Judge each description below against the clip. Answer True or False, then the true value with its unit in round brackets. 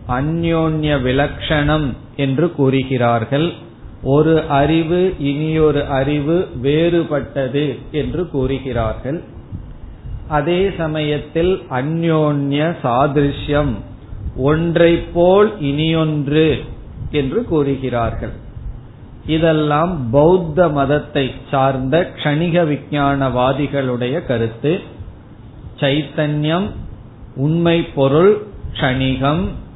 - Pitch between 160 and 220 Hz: False (145 Hz)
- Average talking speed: False (65 wpm)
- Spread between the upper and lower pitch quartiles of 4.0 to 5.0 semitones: False (3.6 semitones)